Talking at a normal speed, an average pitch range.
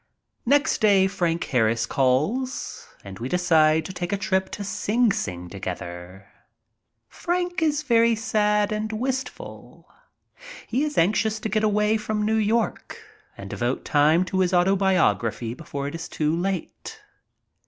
No: average, 145 wpm; wide, 6.2 semitones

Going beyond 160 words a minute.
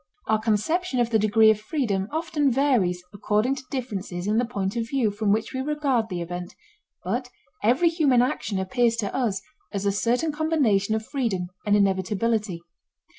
Yes: average, 175 wpm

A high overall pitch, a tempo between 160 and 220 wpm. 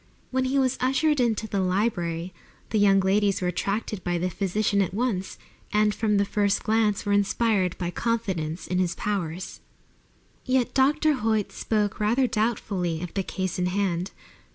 Yes: high, 205 Hz; average, 165 wpm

